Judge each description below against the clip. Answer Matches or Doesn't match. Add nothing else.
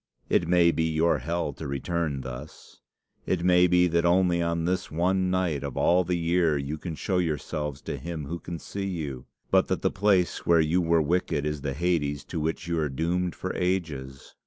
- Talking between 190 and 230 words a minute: Matches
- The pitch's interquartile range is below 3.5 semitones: Matches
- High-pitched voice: Doesn't match